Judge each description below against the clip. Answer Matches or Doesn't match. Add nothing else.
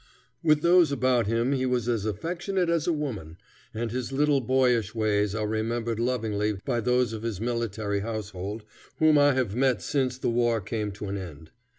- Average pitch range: Matches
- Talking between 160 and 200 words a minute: Matches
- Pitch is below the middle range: Matches